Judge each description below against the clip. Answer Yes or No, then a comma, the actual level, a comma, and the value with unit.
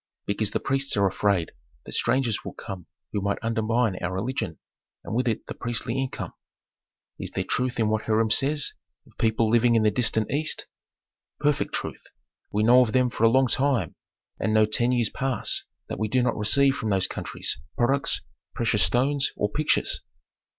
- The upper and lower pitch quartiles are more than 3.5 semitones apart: No, average, 3.2 semitones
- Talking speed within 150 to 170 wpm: No, average, 180 wpm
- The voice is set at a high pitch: No, low, 115 Hz